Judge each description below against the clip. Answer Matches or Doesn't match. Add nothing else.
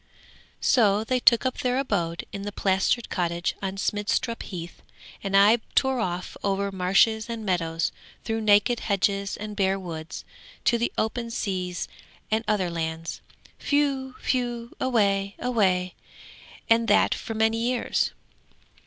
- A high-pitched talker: Matches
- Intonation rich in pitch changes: Doesn't match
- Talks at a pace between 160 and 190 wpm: Doesn't match